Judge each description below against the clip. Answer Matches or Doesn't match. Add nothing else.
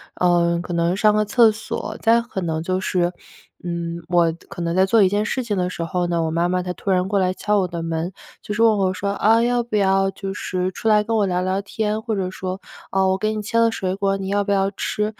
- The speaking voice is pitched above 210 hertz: Doesn't match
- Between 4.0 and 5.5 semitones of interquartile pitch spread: Doesn't match